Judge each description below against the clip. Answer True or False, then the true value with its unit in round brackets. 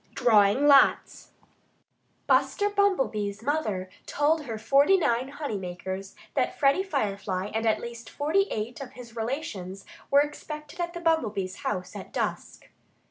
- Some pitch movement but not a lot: False (6.5 semitones)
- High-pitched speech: True (250 Hz)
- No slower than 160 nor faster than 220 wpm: False (140 wpm)